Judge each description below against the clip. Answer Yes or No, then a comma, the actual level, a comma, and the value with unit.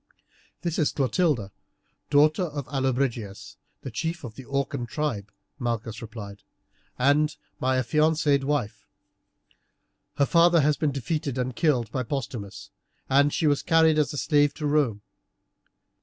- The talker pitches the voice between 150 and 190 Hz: No, medium, 140 Hz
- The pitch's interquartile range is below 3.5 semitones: No, average, 4.1 semitones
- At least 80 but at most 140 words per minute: Yes, slow, 135 wpm